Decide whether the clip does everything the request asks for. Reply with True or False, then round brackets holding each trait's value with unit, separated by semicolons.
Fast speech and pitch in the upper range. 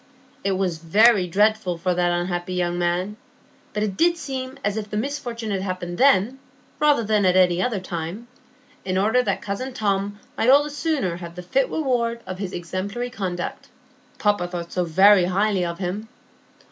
False (175 wpm; 200 Hz)